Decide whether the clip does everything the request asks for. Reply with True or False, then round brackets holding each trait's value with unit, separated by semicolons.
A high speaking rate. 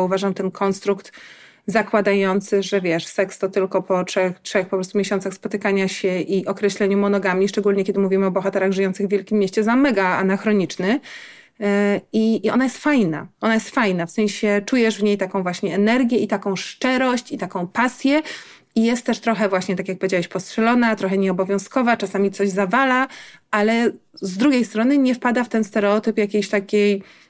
True (175 wpm)